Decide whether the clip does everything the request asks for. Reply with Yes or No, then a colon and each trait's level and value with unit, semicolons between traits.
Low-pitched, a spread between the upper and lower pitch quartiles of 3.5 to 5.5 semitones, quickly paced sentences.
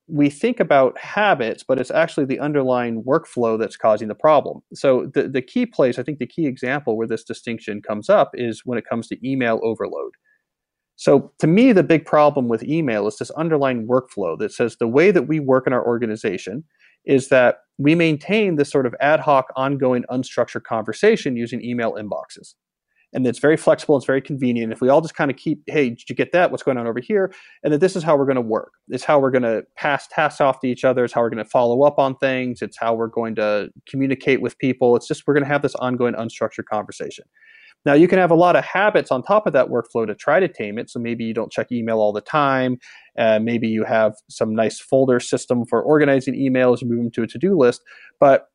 Yes: low, 130 Hz; average, 4.0 semitones; fast, 235 wpm